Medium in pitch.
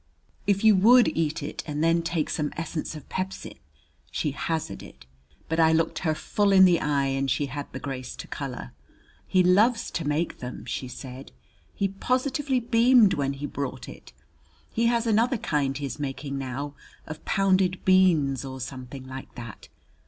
Yes: medium, 155 Hz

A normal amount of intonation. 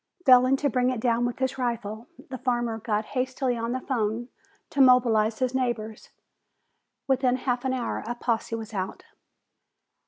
No: narrow, 2.2 semitones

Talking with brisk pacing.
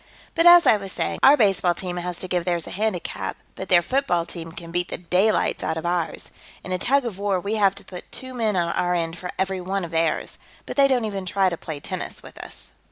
Yes: fast, 250 wpm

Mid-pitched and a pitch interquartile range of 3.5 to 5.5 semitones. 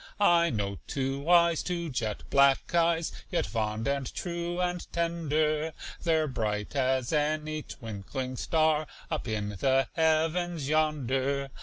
Yes: medium, 150 Hz; average, 4.1 semitones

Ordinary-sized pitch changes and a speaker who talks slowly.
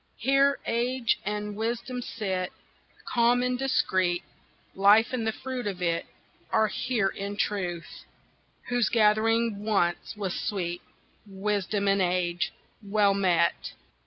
Yes: average, 3.6 semitones; slow, 120 wpm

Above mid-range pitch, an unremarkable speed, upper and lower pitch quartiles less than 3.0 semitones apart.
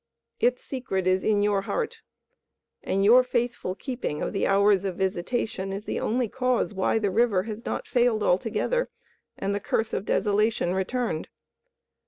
No: high, 210 Hz; average, 160 wpm; average, 4.0 semitones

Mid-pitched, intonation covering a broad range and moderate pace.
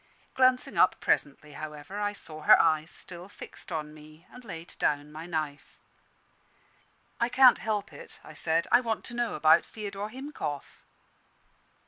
Yes: medium, 170 Hz; wide, 6.2 semitones; average, 150 wpm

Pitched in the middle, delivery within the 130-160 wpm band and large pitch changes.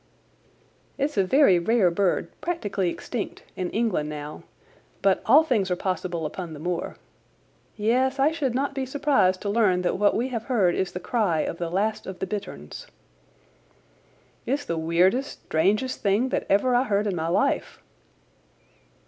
No: high, 200 Hz; average, 155 wpm; wide, 6.0 semitones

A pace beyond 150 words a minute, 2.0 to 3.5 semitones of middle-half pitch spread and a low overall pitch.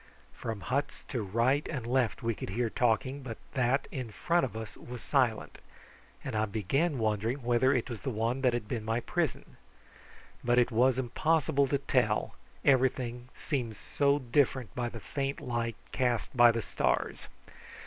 Yes: average, 170 wpm; average, 2.8 semitones; low, 125 Hz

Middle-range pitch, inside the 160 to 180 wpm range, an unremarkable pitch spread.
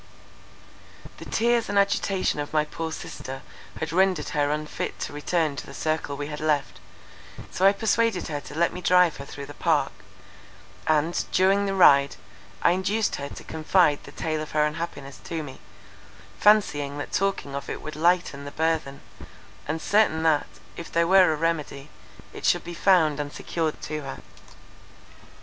Yes: medium, 160 Hz; average, 170 wpm; average, 3.7 semitones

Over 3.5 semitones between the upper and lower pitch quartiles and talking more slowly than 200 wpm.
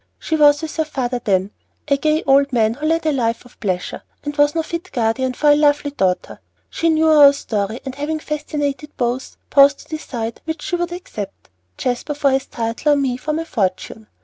No: average, 4.1 semitones; fast, 205 wpm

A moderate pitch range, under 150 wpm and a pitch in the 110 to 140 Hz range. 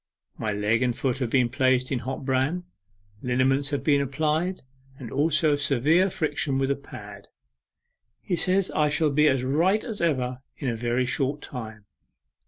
No: average, 3.3 semitones; average, 170 wpm; low, 135 Hz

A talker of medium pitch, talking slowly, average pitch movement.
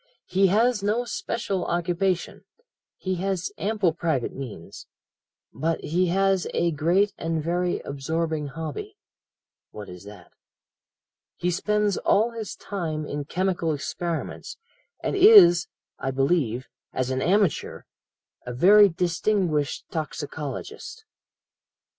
Yes: medium, 175 Hz; slow, 110 wpm; average, 4.7 semitones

